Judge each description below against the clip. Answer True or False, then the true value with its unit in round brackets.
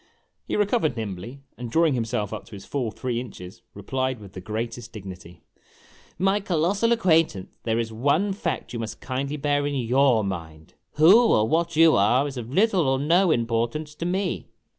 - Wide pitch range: True (6.6 semitones)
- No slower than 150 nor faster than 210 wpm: True (185 wpm)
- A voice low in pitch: True (130 Hz)